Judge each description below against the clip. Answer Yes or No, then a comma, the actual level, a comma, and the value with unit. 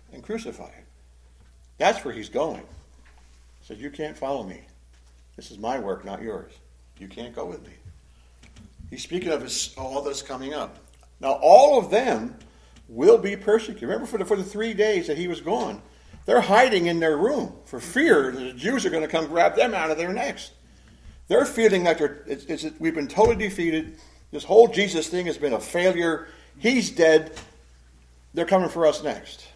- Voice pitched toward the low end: No, medium, 150 Hz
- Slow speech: No, average, 195 wpm